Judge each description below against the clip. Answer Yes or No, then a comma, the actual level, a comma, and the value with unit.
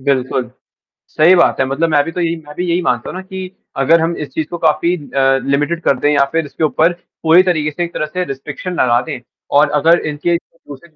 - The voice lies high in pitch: No, medium, 160 Hz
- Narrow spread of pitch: No, average, 3.1 semitones